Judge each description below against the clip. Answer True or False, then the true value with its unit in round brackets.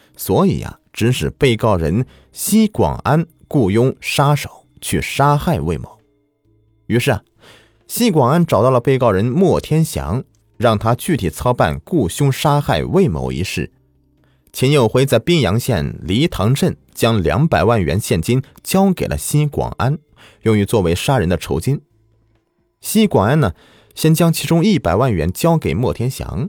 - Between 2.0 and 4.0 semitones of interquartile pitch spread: False (5.2 semitones)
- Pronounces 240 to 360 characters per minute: False (225 characters per minute)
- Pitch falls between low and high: False (125 Hz)